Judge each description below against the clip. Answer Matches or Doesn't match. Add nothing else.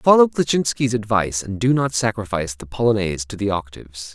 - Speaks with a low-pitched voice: Matches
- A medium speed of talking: Matches